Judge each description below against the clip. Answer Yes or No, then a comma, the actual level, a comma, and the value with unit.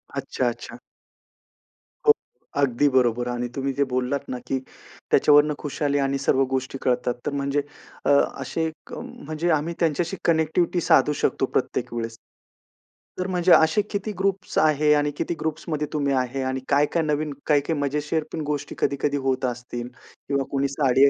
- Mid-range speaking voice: Yes, medium, 145 Hz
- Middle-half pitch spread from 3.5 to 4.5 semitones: No, average, 2.8 semitones